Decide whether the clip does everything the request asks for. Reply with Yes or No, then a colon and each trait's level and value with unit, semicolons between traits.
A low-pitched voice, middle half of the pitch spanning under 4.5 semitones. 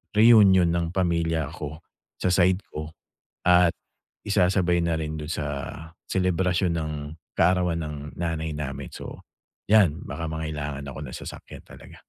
Yes: very low, 85 Hz; average, 2.8 semitones